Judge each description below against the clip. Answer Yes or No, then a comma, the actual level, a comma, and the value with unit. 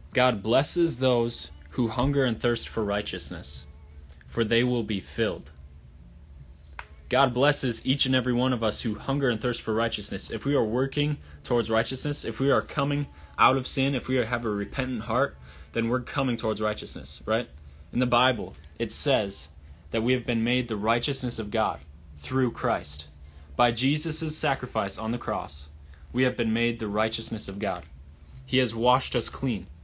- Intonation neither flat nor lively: No, wide, 8.3 semitones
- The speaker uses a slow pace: No, average, 175 wpm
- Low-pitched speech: Yes, low, 115 Hz